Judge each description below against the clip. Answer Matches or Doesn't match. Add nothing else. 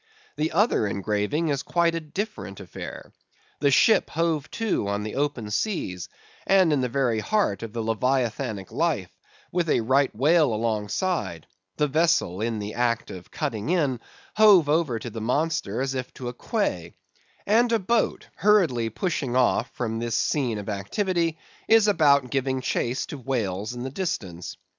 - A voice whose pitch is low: Matches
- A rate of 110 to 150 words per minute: Doesn't match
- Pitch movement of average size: Doesn't match